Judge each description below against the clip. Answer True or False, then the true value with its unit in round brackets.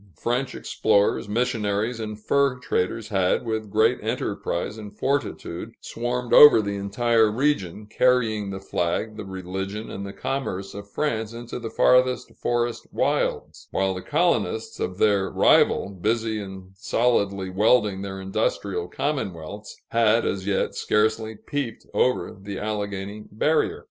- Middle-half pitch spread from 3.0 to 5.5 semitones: True (3.3 semitones)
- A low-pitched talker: True (105 Hz)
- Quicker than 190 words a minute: False (135 wpm)